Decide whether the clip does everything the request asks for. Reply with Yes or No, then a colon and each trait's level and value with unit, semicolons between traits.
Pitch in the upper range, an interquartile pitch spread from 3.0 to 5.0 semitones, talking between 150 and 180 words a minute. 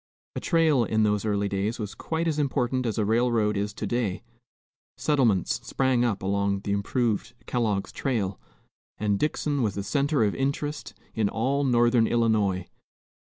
No: low, 115 Hz; average, 4.4 semitones; average, 160 wpm